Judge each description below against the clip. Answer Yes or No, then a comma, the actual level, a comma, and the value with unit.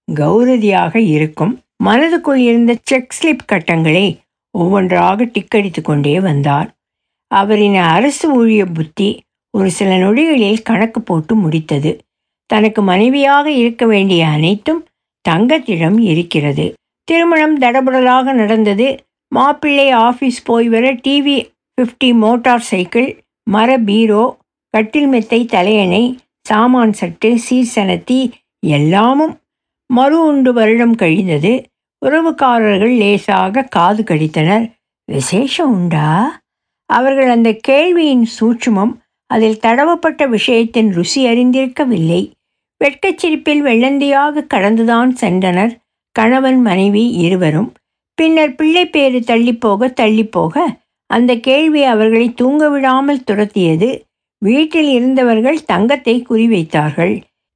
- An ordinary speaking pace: Yes, average, 90 wpm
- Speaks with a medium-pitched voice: No, high, 230 Hz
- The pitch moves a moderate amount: Yes, average, 4.6 semitones